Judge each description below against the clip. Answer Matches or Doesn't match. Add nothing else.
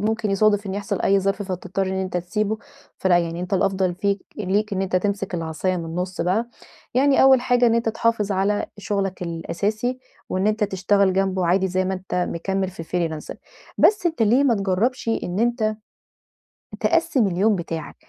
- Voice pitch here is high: Matches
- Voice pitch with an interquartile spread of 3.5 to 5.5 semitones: Doesn't match